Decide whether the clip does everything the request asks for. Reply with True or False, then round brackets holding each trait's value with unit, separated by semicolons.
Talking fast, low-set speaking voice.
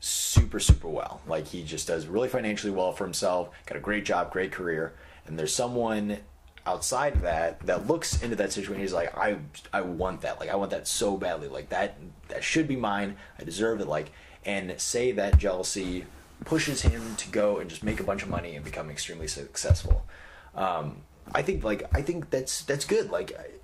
True (210 wpm; 95 Hz)